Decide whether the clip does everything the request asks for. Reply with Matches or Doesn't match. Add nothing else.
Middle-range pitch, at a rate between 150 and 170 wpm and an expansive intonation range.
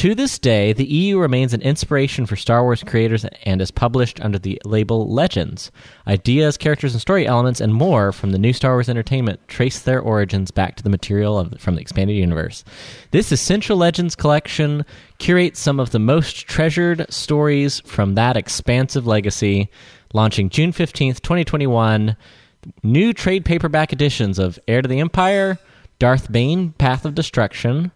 Doesn't match